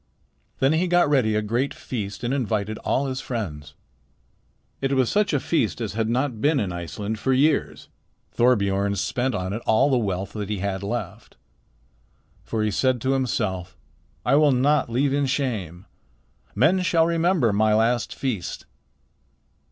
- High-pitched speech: No, low, 120 Hz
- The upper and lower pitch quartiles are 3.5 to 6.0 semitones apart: Yes, average, 4.9 semitones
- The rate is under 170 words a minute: Yes, average, 160 wpm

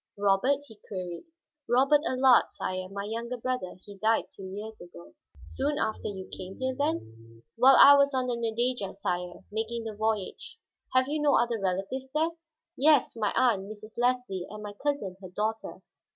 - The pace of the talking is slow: No, average, 170 wpm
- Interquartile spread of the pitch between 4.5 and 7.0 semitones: Yes, average, 4.9 semitones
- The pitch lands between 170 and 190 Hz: No, high, 220 Hz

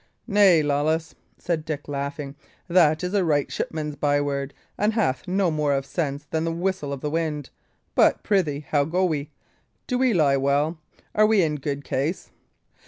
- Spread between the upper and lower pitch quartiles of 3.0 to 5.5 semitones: Yes, average, 3.8 semitones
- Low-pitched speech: No, medium, 155 Hz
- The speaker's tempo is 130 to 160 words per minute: No, average, 170 wpm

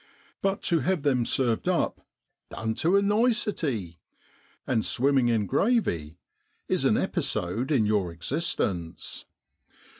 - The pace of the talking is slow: Yes, slow, 125 wpm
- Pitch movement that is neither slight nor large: No, wide, 8.9 semitones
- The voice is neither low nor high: No, low, 125 Hz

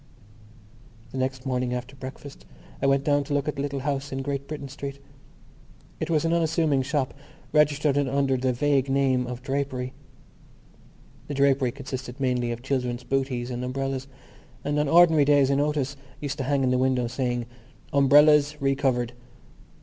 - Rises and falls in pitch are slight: Yes, narrow, 1.9 semitones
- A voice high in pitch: No, low, 135 Hz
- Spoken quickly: No, average, 165 wpm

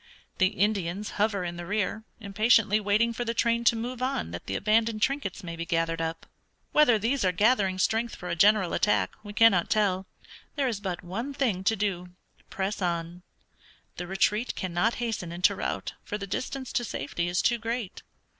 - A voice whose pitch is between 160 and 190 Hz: No, high, 205 Hz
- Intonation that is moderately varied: Yes, average, 4.2 semitones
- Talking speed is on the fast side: No, average, 185 wpm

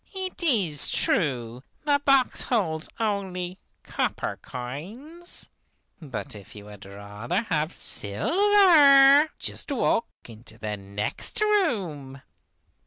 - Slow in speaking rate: Yes, slow, 105 wpm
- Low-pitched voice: No, medium, 180 Hz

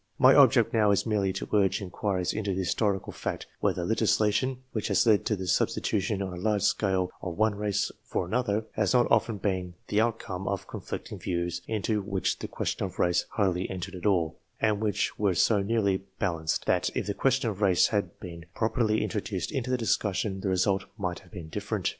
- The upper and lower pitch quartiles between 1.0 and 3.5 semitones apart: Yes, average, 2.7 semitones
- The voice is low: Yes, low, 100 Hz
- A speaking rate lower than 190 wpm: No, average, 200 wpm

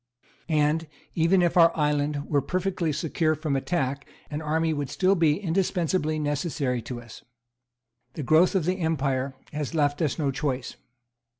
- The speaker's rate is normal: Yes, average, 155 wpm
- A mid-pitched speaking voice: Yes, medium, 155 Hz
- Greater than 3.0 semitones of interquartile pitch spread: No, average, 2.7 semitones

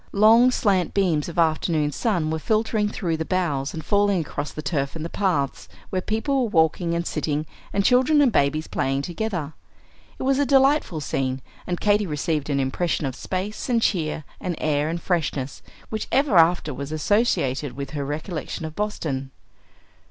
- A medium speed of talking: Yes, average, 175 wpm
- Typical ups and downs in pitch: No, wide, 5.8 semitones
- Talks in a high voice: No, medium, 170 Hz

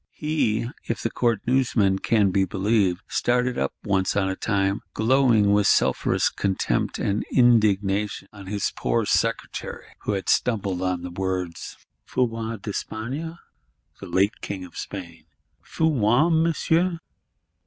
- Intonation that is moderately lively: Yes, average, 4.1 semitones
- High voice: No, low, 105 Hz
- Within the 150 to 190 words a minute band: No, average, 140 wpm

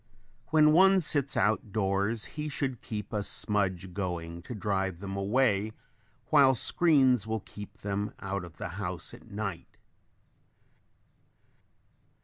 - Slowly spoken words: Yes, slow, 130 wpm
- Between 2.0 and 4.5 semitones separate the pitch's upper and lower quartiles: No, average, 5.2 semitones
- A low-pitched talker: Yes, low, 105 Hz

